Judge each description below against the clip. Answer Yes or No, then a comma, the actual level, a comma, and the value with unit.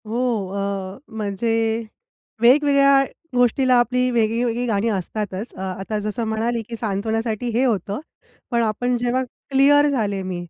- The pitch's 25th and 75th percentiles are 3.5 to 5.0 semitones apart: No, average, 3.0 semitones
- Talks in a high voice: Yes, high, 230 Hz